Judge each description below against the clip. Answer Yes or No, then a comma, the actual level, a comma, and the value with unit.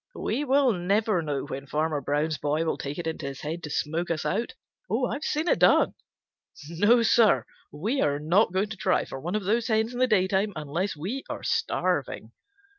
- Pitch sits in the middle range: Yes, medium, 175 Hz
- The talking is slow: No, average, 195 wpm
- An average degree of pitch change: No, wide, 6.5 semitones